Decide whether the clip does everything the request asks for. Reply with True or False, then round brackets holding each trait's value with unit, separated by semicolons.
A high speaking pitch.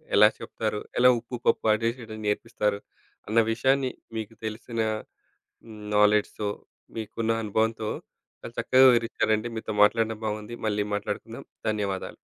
False (110 Hz)